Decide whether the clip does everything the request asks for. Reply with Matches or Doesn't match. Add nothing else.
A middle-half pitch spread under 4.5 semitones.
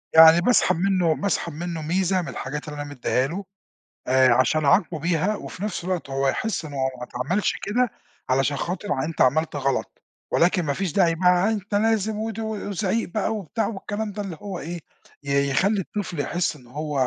Doesn't match